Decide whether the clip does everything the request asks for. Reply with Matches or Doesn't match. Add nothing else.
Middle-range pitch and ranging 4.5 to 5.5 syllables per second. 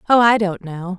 Doesn't match